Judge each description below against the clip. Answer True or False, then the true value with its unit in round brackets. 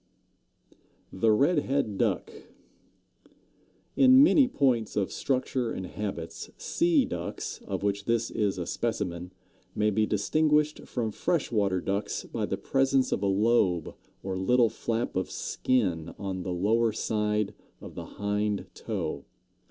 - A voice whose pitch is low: True (105 Hz)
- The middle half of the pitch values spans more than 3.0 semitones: True (4.6 semitones)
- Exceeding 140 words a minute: False (135 wpm)